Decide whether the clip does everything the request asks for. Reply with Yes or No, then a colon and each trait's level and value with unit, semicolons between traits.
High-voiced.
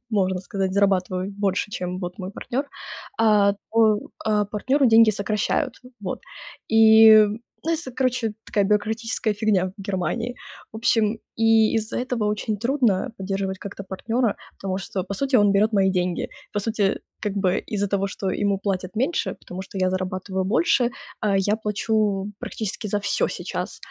Yes: high, 205 Hz